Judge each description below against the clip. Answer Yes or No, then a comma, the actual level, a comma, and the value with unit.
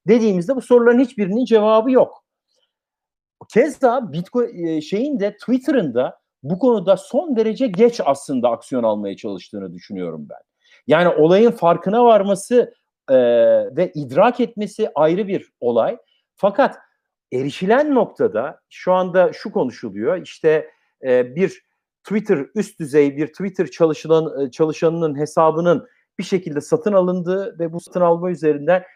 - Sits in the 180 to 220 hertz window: Yes, high, 190 Hz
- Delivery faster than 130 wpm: No, average, 125 wpm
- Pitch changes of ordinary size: No, wide, 7.0 semitones